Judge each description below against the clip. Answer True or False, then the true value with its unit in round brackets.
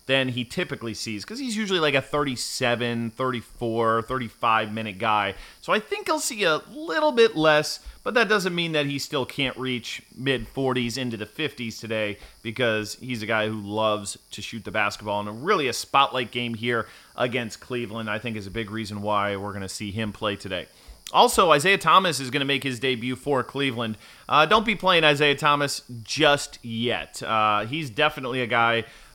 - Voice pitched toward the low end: True (125 Hz)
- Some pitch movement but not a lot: True (4.6 semitones)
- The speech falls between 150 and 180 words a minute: False (195 wpm)